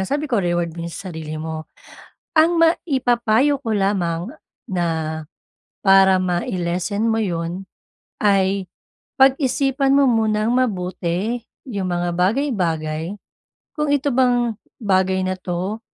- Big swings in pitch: Yes, wide, 5.9 semitones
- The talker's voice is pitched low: No, high, 195 Hz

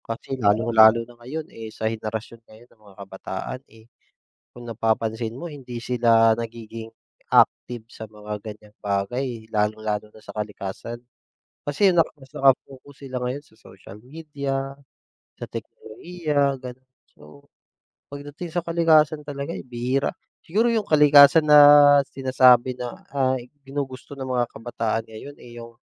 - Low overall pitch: Yes, low, 125 Hz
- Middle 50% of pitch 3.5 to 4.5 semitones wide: Yes, average, 4.1 semitones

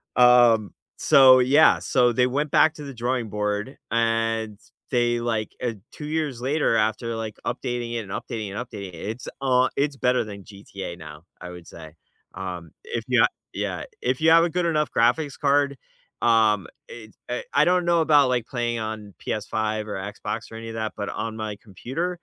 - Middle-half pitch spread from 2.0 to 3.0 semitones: No, average, 3.8 semitones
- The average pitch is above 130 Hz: No, low, 120 Hz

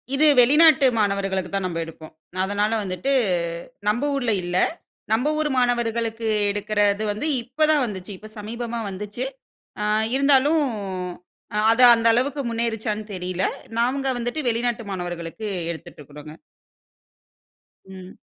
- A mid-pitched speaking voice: No, high, 220 Hz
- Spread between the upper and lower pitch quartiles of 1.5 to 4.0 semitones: No, average, 4.4 semitones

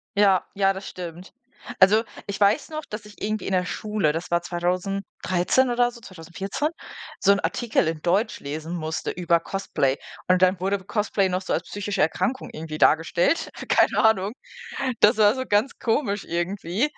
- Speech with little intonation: No, average, 3.3 semitones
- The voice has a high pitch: Yes, high, 195 Hz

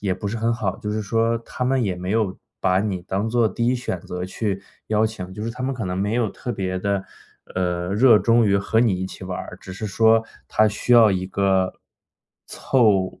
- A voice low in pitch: Yes, low, 105 Hz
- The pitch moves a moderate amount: Yes, average, 3.5 semitones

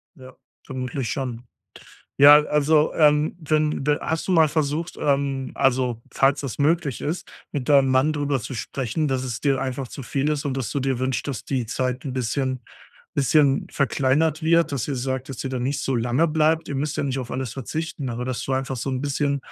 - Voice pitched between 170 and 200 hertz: No, low, 135 Hz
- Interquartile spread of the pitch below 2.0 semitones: No, narrow, 2.4 semitones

